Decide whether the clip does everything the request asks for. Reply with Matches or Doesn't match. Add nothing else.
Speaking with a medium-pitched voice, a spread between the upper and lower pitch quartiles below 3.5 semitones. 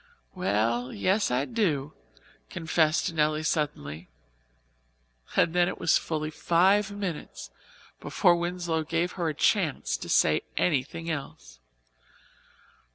Doesn't match